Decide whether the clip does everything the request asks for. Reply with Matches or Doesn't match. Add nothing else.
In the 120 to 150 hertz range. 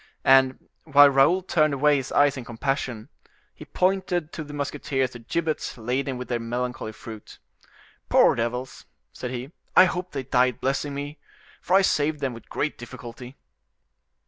Matches